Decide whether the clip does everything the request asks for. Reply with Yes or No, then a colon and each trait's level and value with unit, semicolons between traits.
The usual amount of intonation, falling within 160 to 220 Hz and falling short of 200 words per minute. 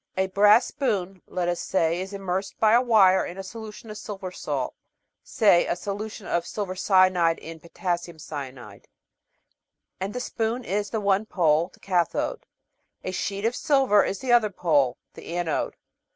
Yes: average, 3.5 semitones; high, 190 Hz; average, 170 wpm